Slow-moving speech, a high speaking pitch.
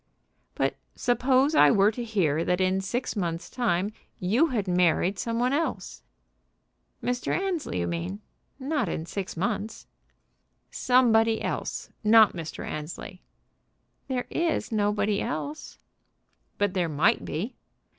Yes: slow, 125 wpm; high, 210 Hz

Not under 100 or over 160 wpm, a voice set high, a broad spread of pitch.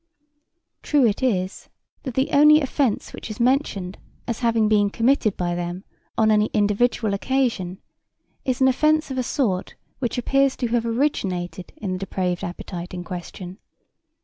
Yes: average, 155 wpm; high, 220 Hz; wide, 5.9 semitones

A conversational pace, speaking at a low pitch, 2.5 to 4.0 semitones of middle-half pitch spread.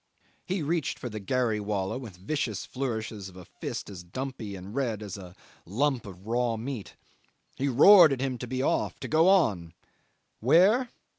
No: average, 175 wpm; low, 120 Hz; wide, 5.5 semitones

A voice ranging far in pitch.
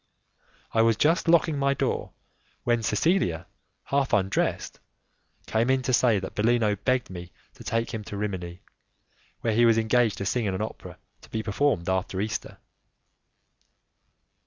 No: average, 3.9 semitones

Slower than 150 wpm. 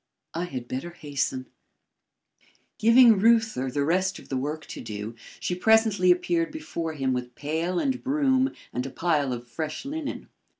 No: average, 160 wpm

